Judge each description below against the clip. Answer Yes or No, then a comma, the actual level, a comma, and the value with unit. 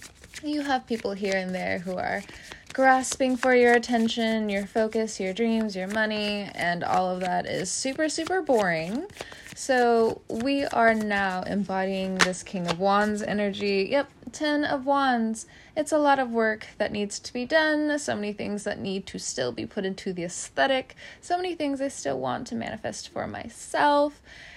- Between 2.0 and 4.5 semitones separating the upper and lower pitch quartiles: No, average, 5.3 semitones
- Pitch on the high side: Yes, high, 220 Hz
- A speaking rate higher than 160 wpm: Yes, average, 175 wpm